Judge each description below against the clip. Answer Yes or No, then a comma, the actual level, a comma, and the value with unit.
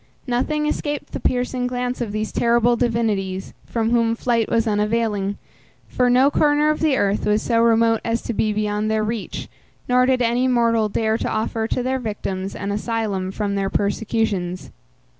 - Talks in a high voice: Yes, high, 230 Hz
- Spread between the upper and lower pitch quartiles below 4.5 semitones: Yes, average, 2.8 semitones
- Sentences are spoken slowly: No, average, 175 wpm